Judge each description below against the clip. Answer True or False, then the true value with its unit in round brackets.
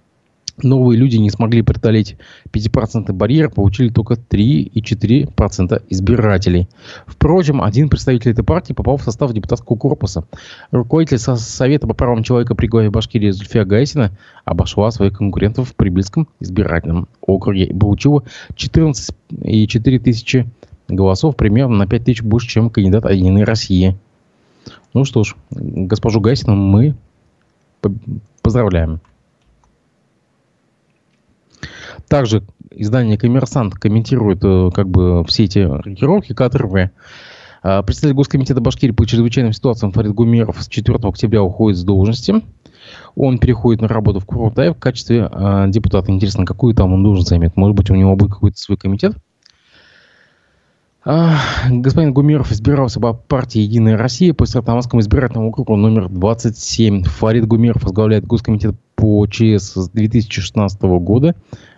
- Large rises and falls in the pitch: False (4.0 semitones)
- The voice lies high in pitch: False (110 Hz)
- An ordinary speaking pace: True (125 wpm)